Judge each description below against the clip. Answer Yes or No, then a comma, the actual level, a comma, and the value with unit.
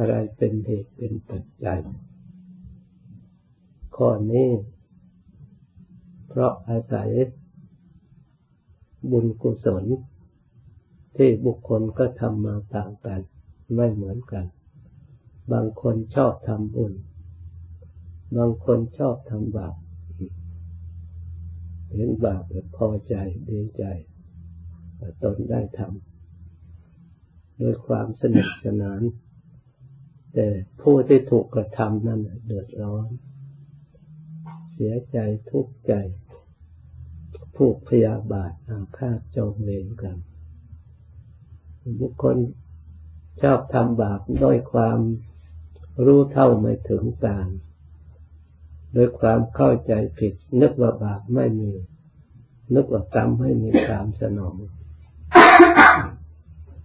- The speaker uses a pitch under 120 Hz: Yes, low, 105 Hz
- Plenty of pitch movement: Yes, wide, 5.7 semitones